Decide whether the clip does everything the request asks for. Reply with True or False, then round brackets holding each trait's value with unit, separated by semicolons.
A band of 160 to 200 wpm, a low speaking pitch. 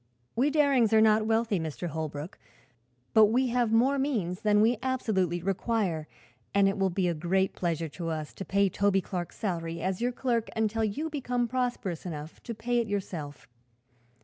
False (175 wpm; 205 Hz)